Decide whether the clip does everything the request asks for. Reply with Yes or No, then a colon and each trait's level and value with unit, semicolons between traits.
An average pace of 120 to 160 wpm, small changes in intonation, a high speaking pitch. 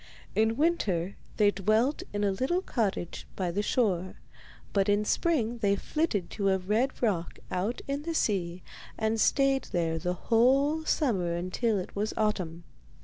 No: average, 155 wpm; average, 5.3 semitones; high, 210 Hz